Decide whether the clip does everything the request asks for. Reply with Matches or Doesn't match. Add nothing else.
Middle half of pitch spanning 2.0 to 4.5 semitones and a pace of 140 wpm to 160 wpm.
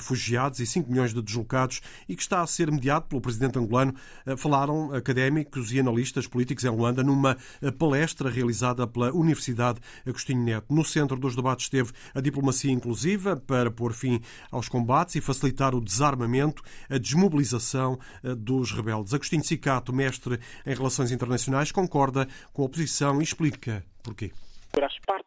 Matches